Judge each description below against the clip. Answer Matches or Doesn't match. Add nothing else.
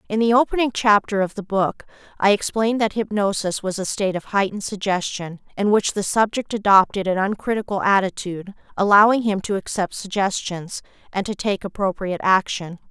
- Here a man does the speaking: Doesn't match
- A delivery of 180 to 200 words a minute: Doesn't match